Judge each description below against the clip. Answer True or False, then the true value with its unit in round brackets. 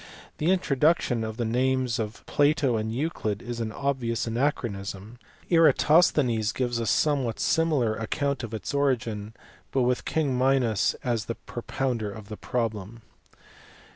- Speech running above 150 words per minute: False (140 wpm)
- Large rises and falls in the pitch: False (3.8 semitones)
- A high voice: False (120 Hz)